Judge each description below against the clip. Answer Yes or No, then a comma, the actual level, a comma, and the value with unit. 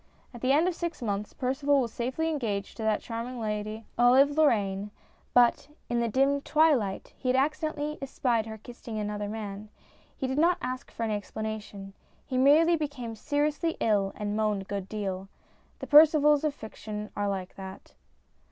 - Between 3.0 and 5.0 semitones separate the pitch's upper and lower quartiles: No, wide, 5.4 semitones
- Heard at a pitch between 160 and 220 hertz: No, high, 235 Hz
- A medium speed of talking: Yes, average, 170 wpm